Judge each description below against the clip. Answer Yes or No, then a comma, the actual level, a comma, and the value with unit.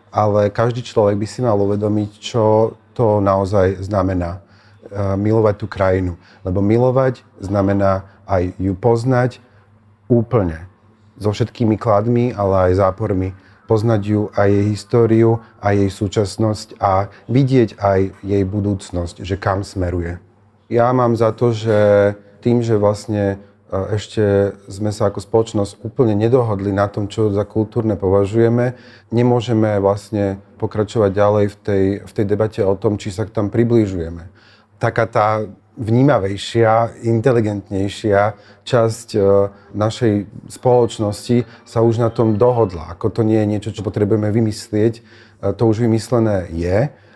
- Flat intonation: Yes, narrow, 2.3 semitones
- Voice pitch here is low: Yes, low, 105 Hz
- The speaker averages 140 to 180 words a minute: No, average, 130 wpm